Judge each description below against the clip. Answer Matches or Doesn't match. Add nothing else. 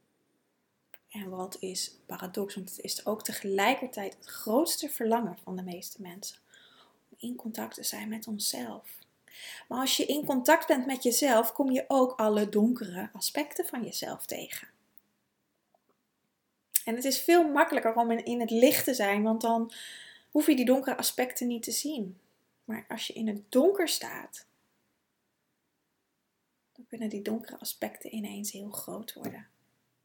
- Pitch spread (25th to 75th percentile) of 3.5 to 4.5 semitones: Matches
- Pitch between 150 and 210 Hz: Doesn't match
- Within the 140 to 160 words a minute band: Matches